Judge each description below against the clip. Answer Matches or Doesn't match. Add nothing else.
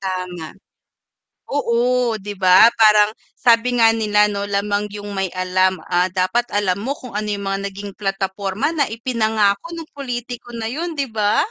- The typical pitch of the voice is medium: Doesn't match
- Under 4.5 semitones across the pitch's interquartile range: Matches